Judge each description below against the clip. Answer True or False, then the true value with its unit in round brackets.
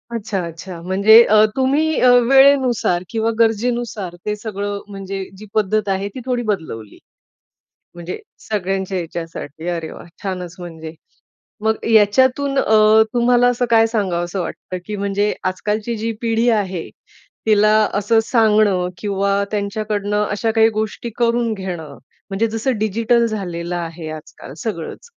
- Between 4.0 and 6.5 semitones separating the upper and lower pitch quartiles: False (3.5 semitones)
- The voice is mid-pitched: False (210 Hz)